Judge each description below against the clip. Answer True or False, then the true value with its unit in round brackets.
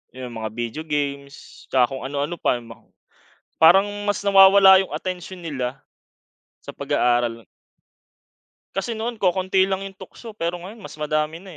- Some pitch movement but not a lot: False (5.9 semitones)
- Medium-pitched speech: True (165 Hz)